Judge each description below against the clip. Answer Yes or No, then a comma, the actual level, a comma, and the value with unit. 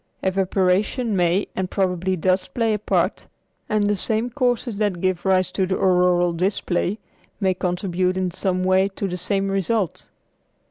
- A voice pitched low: No, high, 190 Hz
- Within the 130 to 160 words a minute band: Yes, average, 155 wpm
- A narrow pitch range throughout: Yes, narrow, 1.9 semitones